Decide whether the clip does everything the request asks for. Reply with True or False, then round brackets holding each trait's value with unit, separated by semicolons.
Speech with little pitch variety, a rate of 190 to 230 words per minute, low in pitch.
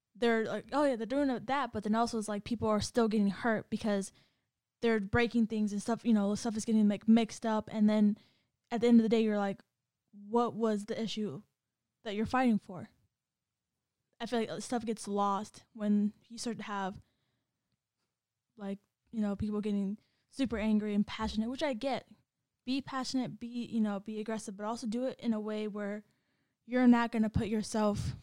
False (2.0 semitones; 200 wpm; 220 Hz)